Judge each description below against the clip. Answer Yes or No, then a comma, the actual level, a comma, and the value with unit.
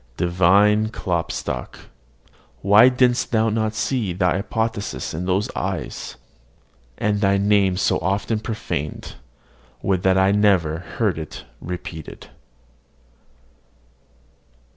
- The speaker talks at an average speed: No, slow, 100 wpm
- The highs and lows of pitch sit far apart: No, average, 3.1 semitones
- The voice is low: Yes, low, 100 Hz